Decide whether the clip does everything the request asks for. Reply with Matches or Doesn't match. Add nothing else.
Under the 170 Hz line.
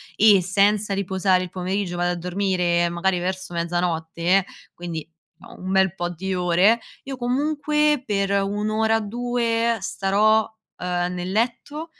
Doesn't match